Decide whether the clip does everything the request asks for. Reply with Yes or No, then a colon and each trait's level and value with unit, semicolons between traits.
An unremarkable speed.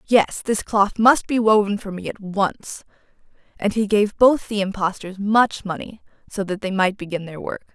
Yes: average, 195 wpm